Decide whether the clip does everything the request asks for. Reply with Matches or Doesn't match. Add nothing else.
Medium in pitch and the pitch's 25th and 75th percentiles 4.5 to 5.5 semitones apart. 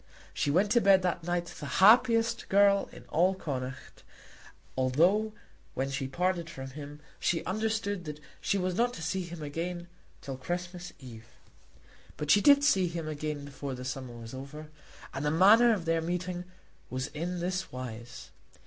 Matches